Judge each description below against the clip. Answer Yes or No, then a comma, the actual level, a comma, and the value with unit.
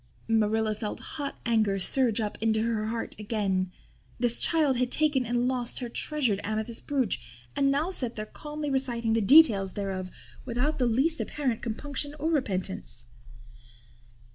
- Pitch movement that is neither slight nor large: Yes, average, 4.4 semitones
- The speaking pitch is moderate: No, high, 235 Hz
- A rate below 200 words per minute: Yes, average, 150 wpm